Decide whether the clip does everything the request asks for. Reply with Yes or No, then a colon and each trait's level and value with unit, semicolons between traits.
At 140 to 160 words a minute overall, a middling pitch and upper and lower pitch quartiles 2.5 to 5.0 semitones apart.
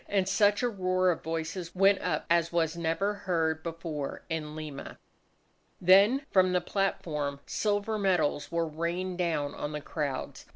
Yes: average, 155 wpm; medium, 170 Hz; average, 3.4 semitones